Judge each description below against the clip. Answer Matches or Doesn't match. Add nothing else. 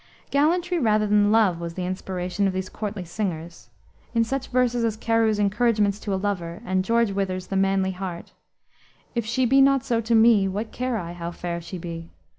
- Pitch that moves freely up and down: Doesn't match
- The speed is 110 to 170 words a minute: Doesn't match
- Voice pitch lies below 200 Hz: Doesn't match